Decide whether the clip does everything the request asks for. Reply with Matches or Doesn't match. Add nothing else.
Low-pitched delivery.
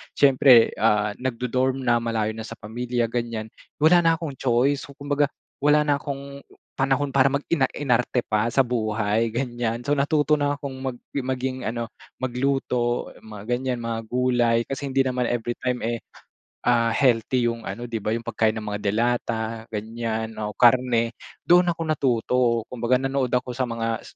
Matches